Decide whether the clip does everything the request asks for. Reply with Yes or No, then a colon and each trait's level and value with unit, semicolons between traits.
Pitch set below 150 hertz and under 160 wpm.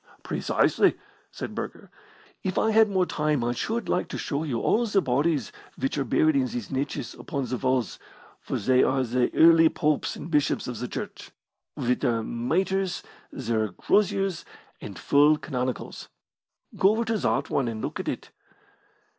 No: medium, 140 Hz; average, 170 wpm